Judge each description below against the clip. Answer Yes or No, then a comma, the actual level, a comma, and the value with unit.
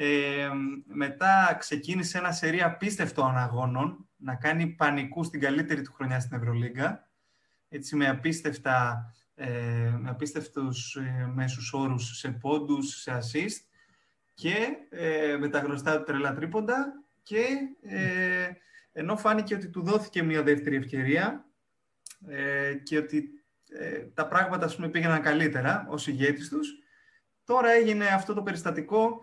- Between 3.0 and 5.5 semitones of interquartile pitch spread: Yes, average, 5.0 semitones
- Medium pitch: Yes, medium, 150 Hz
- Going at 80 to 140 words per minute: Yes, slow, 115 wpm